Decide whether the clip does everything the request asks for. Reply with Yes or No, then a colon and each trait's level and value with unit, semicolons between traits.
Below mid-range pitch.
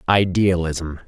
Yes: very low, 90 Hz